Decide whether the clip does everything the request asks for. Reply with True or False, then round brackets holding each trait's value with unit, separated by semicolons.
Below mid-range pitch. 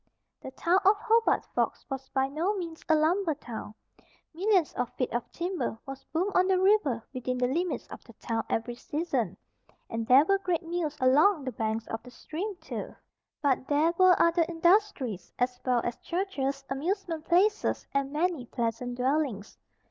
False (300 Hz)